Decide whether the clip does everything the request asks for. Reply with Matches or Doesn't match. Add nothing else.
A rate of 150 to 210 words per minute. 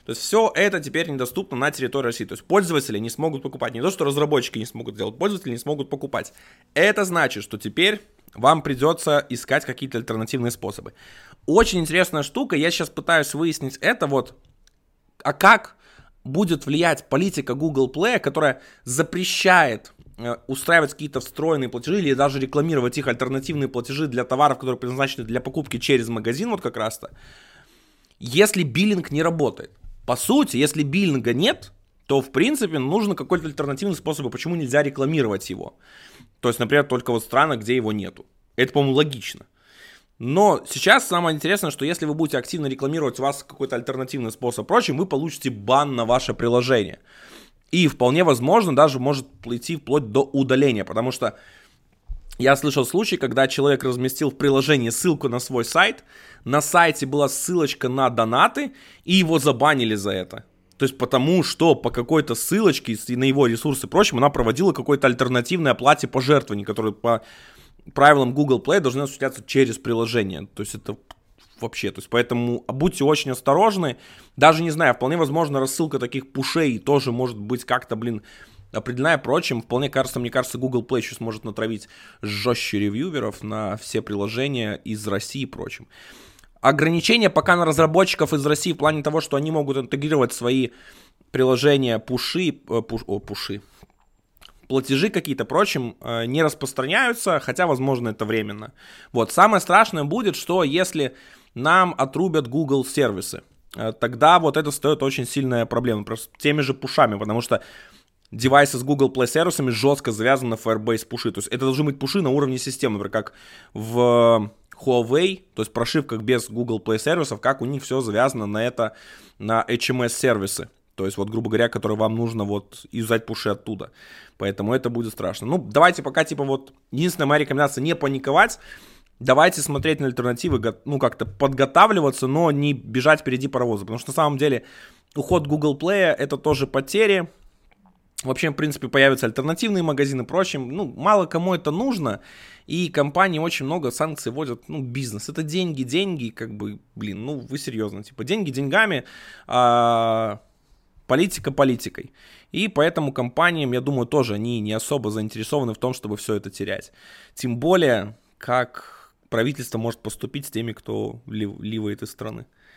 Matches